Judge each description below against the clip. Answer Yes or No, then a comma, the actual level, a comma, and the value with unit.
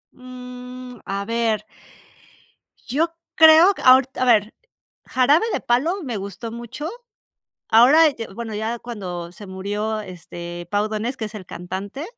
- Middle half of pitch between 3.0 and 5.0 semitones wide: Yes, average, 3.8 semitones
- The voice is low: No, high, 230 Hz